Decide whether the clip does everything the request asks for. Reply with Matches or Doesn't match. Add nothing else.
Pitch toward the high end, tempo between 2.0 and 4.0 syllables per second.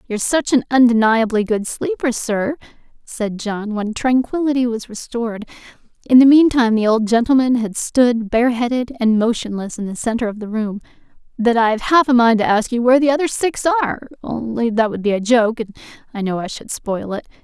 Matches